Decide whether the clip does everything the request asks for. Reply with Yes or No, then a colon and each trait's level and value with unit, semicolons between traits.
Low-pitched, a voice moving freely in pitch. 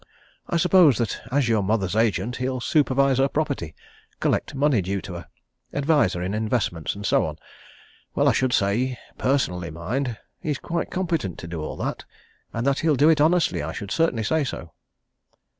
Yes: low, 125 Hz; wide, 6.6 semitones